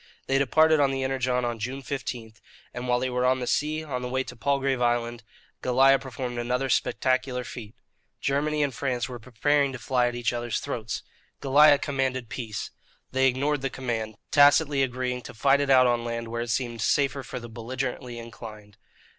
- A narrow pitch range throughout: Yes, narrow, 2.3 semitones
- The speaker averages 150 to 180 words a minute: No, average, 190 wpm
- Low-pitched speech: Yes, low, 125 Hz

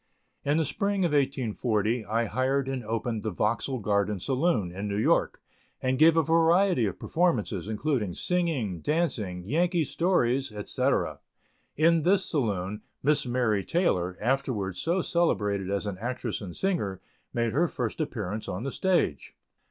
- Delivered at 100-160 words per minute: Yes, average, 150 wpm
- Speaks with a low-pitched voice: Yes, low, 125 Hz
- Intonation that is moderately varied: No, wide, 7.5 semitones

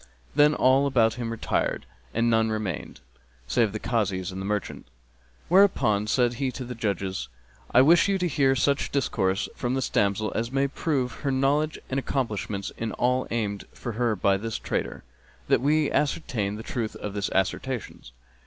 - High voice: No, low, 120 Hz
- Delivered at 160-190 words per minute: Yes, average, 170 wpm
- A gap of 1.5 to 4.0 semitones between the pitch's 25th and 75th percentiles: No, average, 4.5 semitones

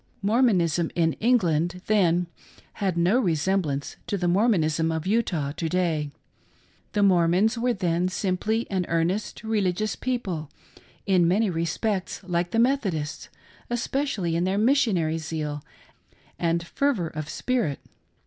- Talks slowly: Yes, slow, 130 wpm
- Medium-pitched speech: Yes, medium, 180 Hz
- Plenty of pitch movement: No, average, 4.6 semitones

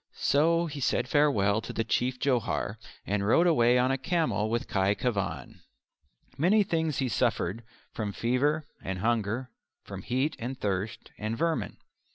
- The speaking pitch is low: Yes, low, 125 Hz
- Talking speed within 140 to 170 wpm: Yes, average, 155 wpm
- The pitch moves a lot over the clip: Yes, wide, 5.9 semitones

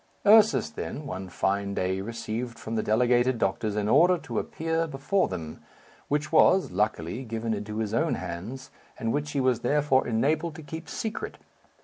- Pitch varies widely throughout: Yes, wide, 5.7 semitones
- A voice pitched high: No, low, 120 Hz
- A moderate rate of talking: Yes, average, 165 wpm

